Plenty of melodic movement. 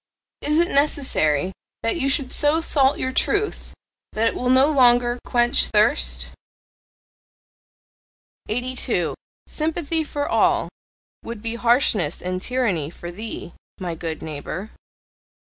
Yes: wide, 7.3 semitones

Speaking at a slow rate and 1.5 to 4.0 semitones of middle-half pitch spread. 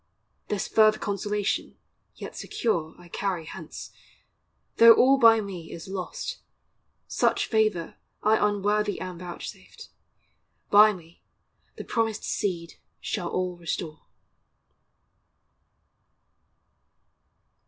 Yes: slow, 95 wpm; average, 3.6 semitones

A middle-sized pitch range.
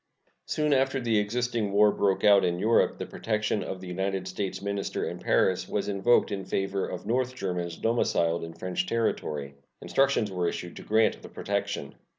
Yes: average, 3.9 semitones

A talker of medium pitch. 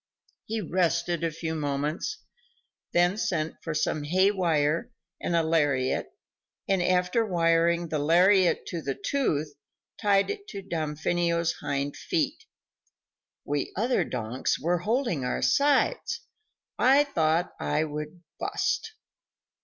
Yes: medium, 170 Hz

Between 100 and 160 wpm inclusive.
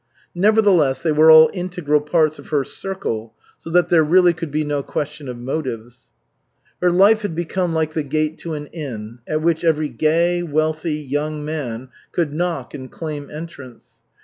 No: average, 175 wpm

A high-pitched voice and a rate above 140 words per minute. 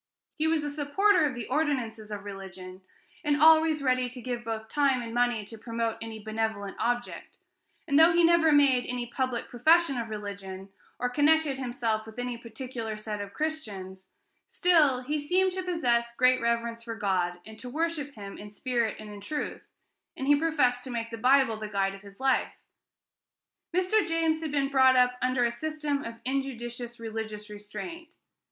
Yes: high, 245 Hz; average, 180 wpm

